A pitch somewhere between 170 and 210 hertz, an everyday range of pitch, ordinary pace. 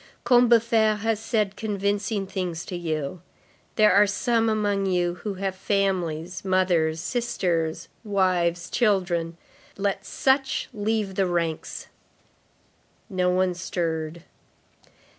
No: high, 190 Hz; average, 3.4 semitones; slow, 105 wpm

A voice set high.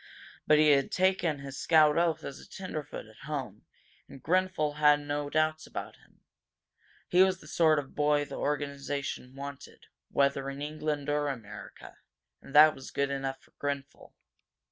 No: medium, 145 Hz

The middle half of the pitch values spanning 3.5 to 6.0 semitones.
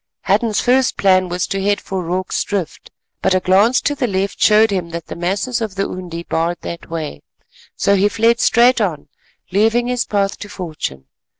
Yes: average, 3.8 semitones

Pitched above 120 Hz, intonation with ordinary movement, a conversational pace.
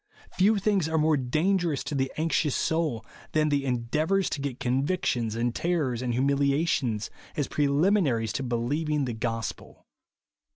Yes: medium, 140 Hz; average, 4.6 semitones; average, 155 wpm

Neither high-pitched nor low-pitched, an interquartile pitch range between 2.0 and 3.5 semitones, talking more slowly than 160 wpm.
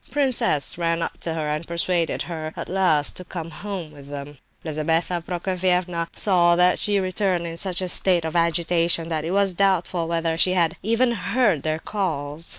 No: medium, 170 Hz; narrow, 2.4 semitones; average, 185 wpm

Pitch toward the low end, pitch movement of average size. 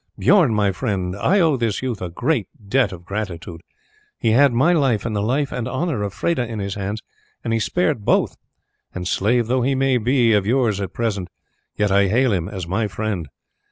Yes: low, 110 Hz; average, 4.7 semitones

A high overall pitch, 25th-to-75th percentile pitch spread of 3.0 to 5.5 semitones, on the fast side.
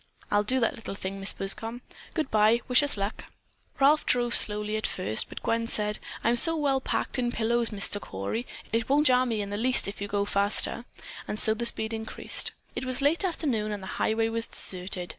Yes: high, 225 Hz; average, 3.4 semitones; fast, 210 wpm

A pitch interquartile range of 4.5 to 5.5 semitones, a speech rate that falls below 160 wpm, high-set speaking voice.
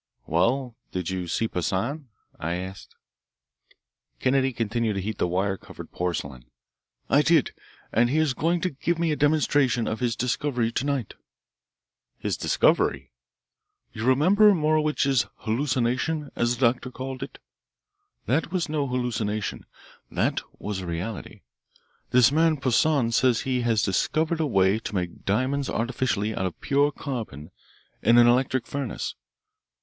No: average, 4.9 semitones; average, 145 wpm; low, 125 Hz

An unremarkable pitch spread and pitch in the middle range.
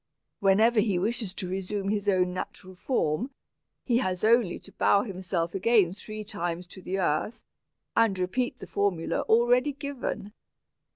No: average, 3.8 semitones; high, 200 Hz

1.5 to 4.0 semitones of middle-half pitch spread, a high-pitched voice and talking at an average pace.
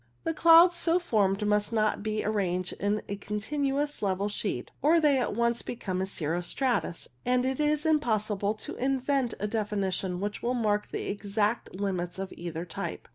No: average, 5.0 semitones; high, 210 Hz; average, 170 wpm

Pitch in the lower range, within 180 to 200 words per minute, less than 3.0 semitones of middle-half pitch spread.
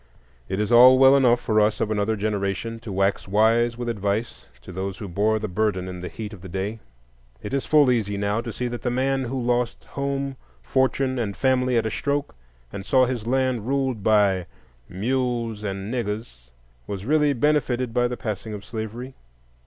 No: low, 115 Hz; average, 190 wpm; average, 3.9 semitones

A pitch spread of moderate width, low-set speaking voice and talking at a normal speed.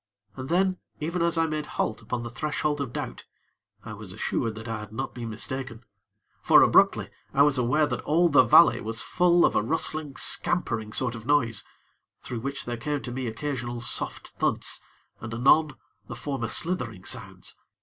Yes: average, 4.7 semitones; low, 130 Hz; average, 180 wpm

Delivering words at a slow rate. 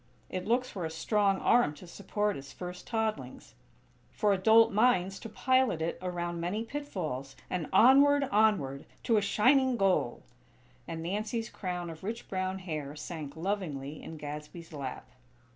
No: average, 150 wpm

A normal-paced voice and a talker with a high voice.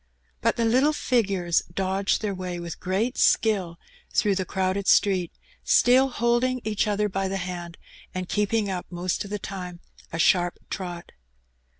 Yes: average, 160 wpm; high, 195 Hz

